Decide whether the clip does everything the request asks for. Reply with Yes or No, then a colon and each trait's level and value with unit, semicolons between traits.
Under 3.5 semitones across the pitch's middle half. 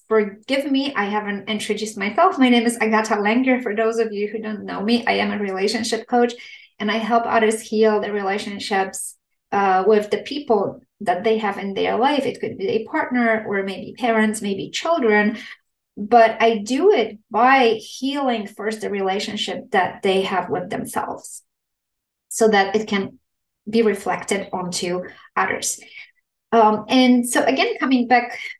Yes: average, 2.8 semitones